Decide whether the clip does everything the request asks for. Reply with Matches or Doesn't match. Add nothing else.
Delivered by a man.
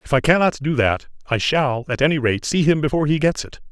Matches